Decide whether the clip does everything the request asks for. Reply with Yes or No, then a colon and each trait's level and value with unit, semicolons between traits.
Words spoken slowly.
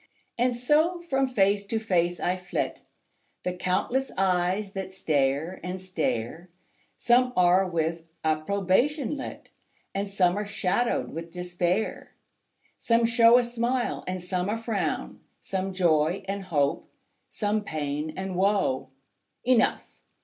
Yes: slow, 130 wpm